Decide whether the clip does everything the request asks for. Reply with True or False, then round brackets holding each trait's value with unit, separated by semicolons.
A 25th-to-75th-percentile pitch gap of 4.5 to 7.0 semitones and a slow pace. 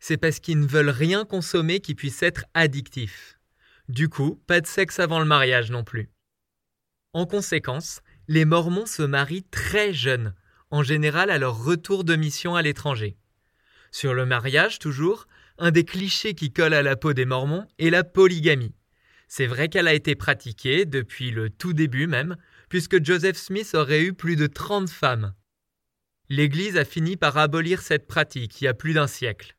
False (5.0 semitones; 180 wpm)